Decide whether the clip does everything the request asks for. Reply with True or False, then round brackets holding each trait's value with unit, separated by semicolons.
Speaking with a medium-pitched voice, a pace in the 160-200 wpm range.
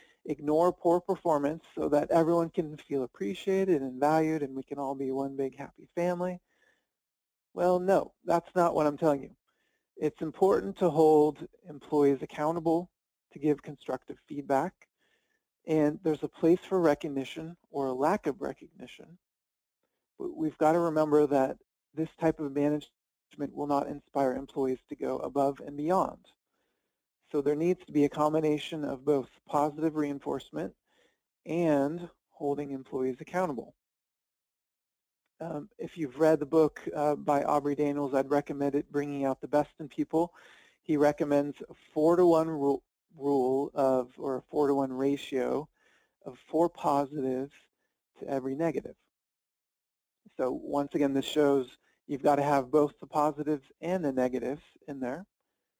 False (150 Hz; 145 wpm)